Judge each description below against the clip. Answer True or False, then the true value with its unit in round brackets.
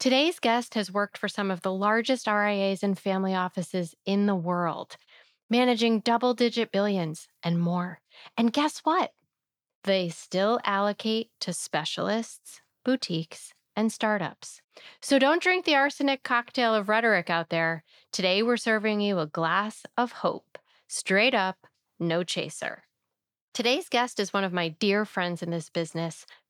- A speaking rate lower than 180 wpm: True (150 wpm)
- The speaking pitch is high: True (205 Hz)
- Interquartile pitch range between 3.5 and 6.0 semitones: True (4.6 semitones)